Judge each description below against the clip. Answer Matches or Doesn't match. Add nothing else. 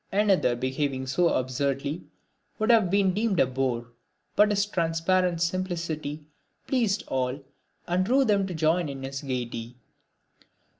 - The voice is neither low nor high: Matches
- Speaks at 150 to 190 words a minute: Doesn't match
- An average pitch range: Doesn't match